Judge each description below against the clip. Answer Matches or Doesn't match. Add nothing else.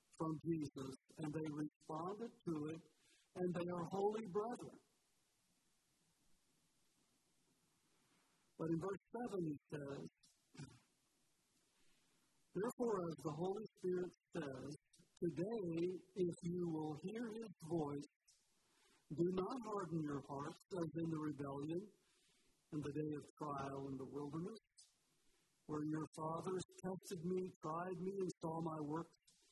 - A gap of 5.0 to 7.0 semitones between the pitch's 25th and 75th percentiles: Doesn't match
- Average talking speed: Doesn't match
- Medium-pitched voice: Matches